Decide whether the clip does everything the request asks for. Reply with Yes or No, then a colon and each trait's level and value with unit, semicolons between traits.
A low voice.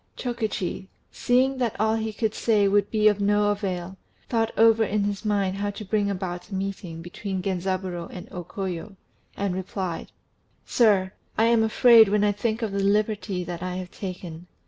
No: high, 200 Hz